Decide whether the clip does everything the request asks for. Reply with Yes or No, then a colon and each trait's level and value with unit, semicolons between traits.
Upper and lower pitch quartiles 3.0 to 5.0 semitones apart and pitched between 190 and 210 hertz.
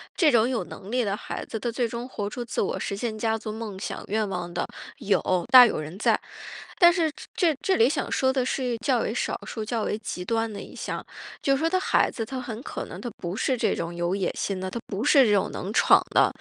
No: average, 4.0 semitones; high, 225 Hz